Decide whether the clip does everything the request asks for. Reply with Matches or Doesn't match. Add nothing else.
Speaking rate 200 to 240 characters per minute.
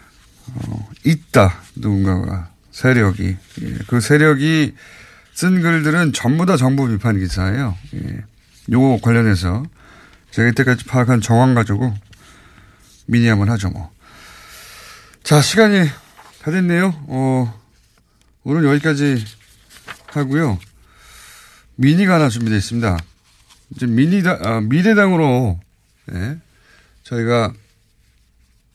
Matches